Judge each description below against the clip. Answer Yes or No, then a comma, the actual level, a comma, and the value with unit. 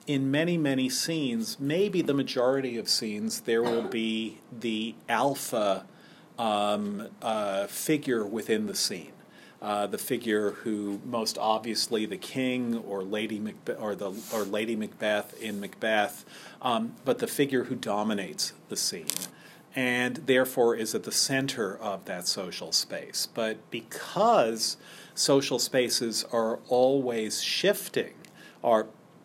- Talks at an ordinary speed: No, slow, 130 wpm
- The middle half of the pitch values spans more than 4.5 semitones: No, average, 3.9 semitones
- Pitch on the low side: Yes, low, 120 Hz